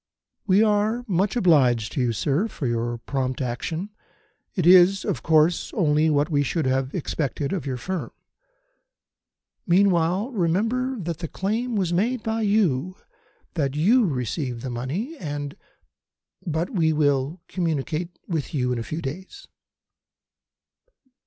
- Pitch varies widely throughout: Yes, wide, 5.9 semitones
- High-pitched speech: No, medium, 165 Hz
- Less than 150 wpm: Yes, average, 140 wpm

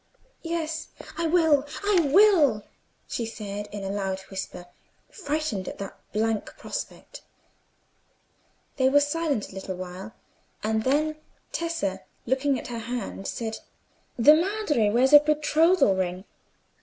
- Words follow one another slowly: Yes, slow, 130 wpm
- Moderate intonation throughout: No, wide, 7.2 semitones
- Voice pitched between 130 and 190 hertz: No, very high, 255 Hz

